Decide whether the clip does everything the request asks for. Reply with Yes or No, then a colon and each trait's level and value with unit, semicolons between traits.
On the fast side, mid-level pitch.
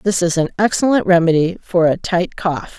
No: average, 195 wpm; medium, 180 Hz